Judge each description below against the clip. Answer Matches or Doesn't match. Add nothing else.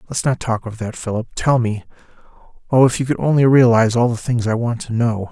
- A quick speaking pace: Matches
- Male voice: Matches